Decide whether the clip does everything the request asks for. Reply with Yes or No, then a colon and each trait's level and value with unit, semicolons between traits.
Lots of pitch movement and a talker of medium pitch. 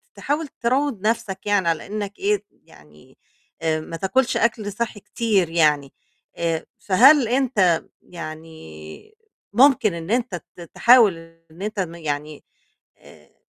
No: wide, 6.3 semitones; high, 200 Hz